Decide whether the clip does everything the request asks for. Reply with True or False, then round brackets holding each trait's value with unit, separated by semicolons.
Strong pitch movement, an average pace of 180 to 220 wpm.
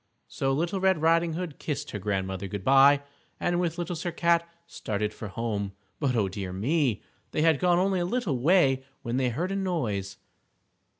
True (8.3 semitones; 190 wpm)